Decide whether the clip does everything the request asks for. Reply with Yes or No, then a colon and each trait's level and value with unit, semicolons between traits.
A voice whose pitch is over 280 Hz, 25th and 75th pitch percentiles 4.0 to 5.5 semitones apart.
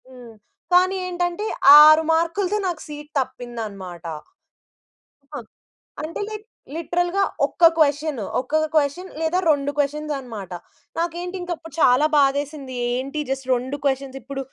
Yes: very high, 295 Hz; average, 4.3 semitones